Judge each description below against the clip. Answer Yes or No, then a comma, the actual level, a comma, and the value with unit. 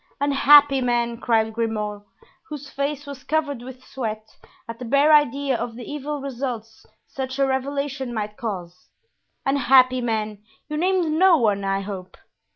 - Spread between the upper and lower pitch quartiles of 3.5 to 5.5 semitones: Yes, average, 4.1 semitones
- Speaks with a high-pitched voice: Yes, very high, 255 Hz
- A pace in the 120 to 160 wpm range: Yes, average, 150 wpm